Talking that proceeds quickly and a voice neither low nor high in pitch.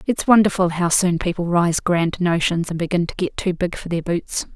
Yes: fast, 225 wpm; medium, 175 Hz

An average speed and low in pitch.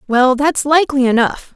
No: average, 155 wpm; very high, 270 Hz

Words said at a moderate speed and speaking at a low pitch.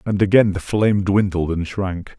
Yes: average, 190 wpm; very low, 95 Hz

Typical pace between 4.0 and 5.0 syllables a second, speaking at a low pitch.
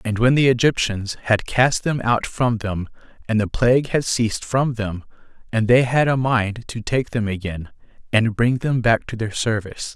Yes: 4.7 syllables/s; low, 115 Hz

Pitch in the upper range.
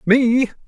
Yes: high, 235 Hz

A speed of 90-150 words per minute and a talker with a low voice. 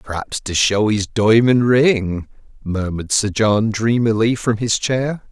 Yes: average, 145 wpm; low, 110 Hz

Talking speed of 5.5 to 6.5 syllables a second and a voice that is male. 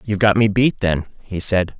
No: 5.2 syllables/s; male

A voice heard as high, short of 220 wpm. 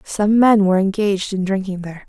Yes: high, 195 Hz; average, 200 wpm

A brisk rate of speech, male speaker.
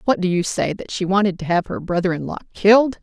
No: fast, 260 wpm; female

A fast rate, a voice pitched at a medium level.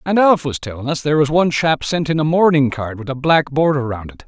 Yes: fast, 280 wpm; medium, 145 Hz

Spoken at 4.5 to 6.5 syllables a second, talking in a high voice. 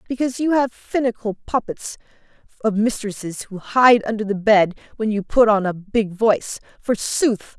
Yes: 4.9 syllables/s; high, 220 Hz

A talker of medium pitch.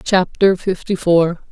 Yes: medium, 180 Hz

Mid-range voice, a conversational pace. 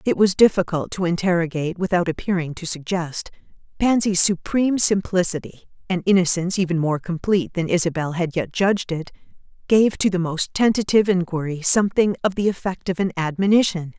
Yes: medium, 180 Hz; average, 155 wpm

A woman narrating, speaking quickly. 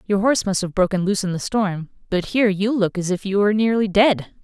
Yes: female; fast, 255 wpm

